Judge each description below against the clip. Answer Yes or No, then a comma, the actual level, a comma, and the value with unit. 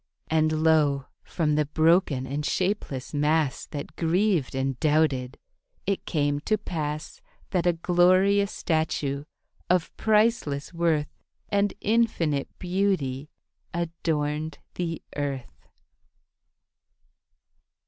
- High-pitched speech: No, medium, 160 Hz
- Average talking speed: No, slow, 95 wpm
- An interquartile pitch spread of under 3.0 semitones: No, average, 3.7 semitones